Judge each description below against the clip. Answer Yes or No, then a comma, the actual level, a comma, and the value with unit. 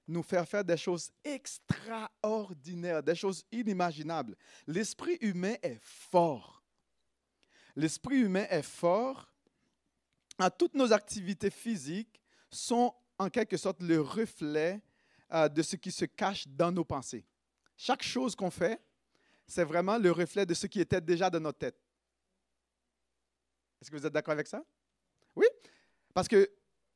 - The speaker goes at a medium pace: No, slow, 135 wpm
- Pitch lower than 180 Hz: No, medium, 185 Hz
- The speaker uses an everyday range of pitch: Yes, average, 4.9 semitones